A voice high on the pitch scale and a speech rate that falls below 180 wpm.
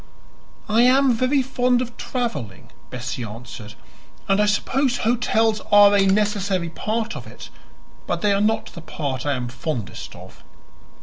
Yes: high, 205 Hz; average, 150 wpm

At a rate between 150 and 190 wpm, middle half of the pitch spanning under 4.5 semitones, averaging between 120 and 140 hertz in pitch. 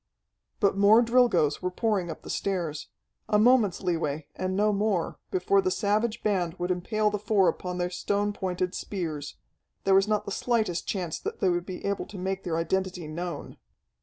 No: average, 185 wpm; average, 3.0 semitones; high, 190 Hz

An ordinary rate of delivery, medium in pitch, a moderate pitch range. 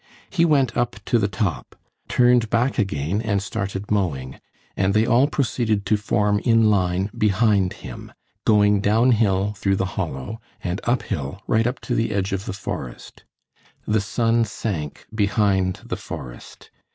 No: average, 150 wpm; low, 105 Hz; average, 3.0 semitones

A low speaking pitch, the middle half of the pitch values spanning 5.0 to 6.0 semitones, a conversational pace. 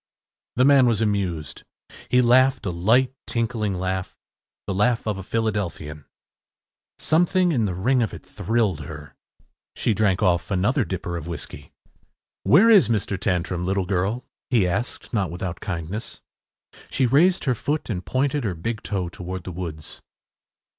Yes: low, 100 Hz; wide, 5.5 semitones; average, 155 wpm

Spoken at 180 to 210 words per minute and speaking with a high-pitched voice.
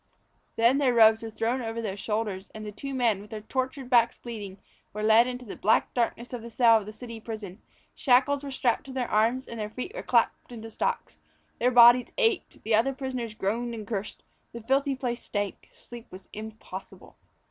Yes: fast, 205 wpm; high, 230 Hz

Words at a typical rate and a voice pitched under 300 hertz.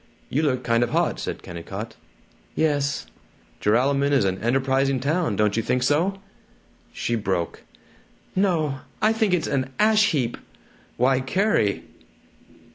No: slow, 130 wpm; low, 135 Hz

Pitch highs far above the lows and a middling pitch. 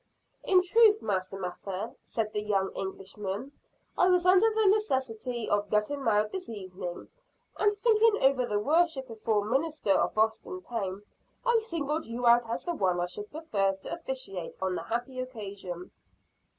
No: wide, 8.6 semitones; high, 230 Hz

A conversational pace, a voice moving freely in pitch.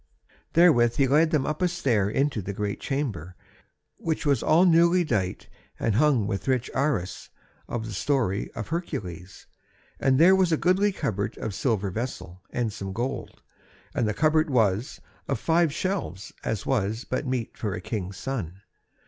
Yes: average, 165 wpm; wide, 7.2 semitones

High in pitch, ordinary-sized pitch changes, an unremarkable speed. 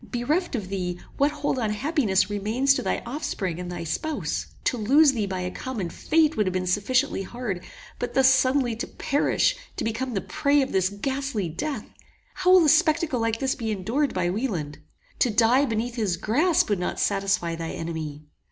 No: high, 230 Hz; wide, 6.6 semitones; average, 190 wpm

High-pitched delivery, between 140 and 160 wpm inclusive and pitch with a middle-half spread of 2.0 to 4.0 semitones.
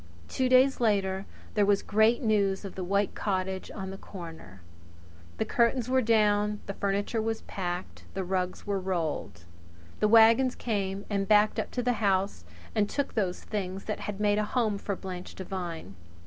No: high, 200 Hz; average, 175 wpm; narrow, 2.4 semitones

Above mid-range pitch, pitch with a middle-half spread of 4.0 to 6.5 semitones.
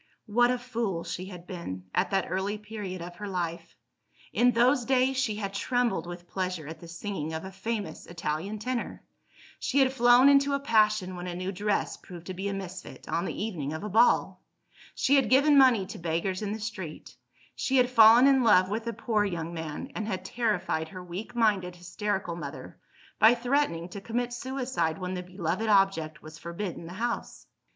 Yes: high, 200 Hz; average, 5.2 semitones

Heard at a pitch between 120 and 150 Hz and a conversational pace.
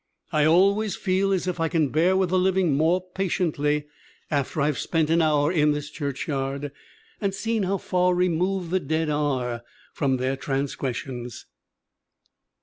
No: medium, 160 Hz; average, 150 wpm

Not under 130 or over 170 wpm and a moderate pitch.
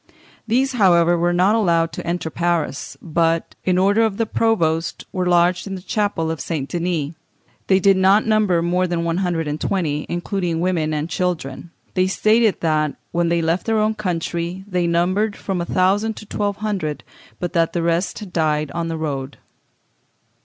No: average, 180 wpm; medium, 175 Hz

